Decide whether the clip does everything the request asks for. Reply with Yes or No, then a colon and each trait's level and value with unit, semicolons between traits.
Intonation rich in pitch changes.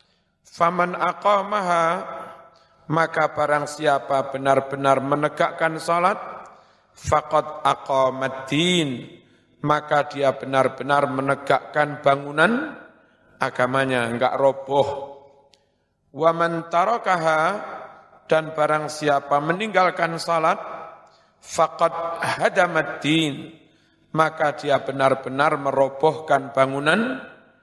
No: average, 3.2 semitones